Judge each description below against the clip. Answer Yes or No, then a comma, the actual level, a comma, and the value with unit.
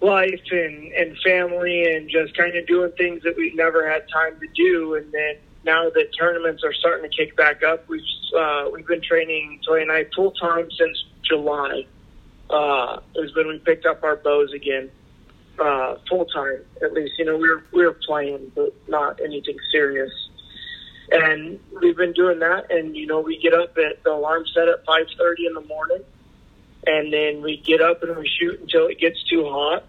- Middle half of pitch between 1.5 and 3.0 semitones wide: Yes, narrow, 2.5 semitones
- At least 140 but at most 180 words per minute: No, average, 195 wpm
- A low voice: No, medium, 165 Hz